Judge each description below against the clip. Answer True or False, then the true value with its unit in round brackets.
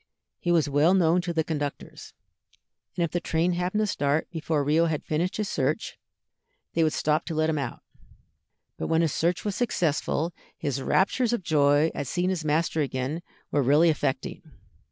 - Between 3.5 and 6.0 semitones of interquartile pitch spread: False (3.0 semitones)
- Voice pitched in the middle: True (160 Hz)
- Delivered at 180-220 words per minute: True (185 wpm)